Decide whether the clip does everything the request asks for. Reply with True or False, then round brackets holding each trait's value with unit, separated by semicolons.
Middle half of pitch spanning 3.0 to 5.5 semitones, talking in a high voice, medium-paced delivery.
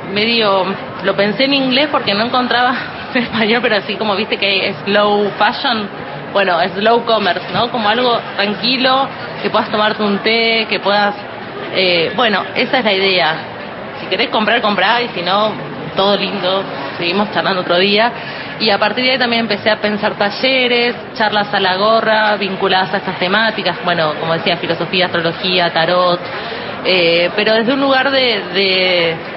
True (3.4 semitones; 205 Hz; 170 wpm)